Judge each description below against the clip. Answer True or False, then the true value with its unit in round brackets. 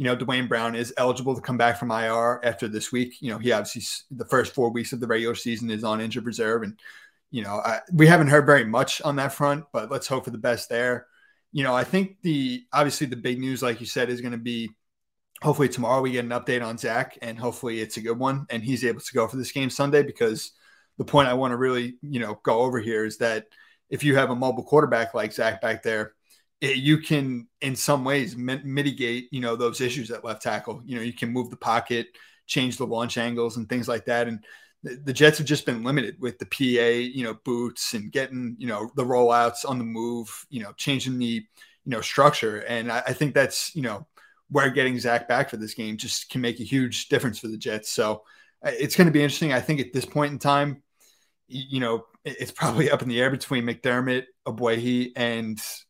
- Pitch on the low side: True (125 Hz)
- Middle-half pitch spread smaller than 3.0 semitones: True (2.4 semitones)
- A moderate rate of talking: False (235 wpm)